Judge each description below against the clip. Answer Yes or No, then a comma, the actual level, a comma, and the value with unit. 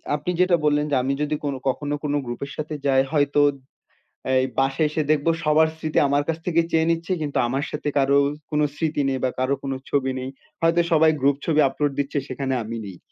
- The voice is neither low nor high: Yes, medium, 145 Hz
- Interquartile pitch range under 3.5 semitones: Yes, narrow, 2.4 semitones